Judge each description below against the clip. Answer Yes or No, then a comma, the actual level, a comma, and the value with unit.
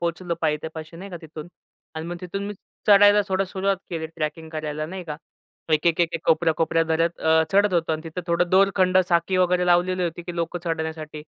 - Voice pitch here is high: No, medium, 170 Hz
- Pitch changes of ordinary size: No, narrow, 2.3 semitones